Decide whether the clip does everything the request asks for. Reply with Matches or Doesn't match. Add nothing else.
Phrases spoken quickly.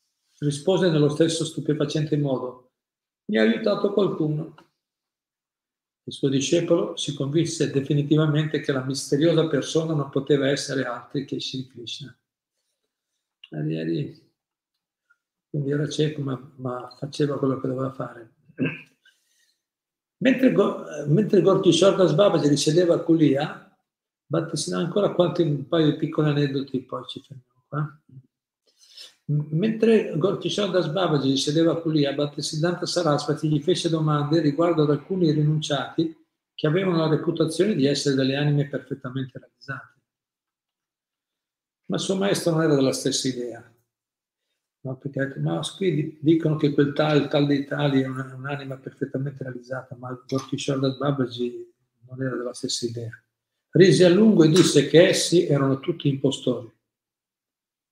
Doesn't match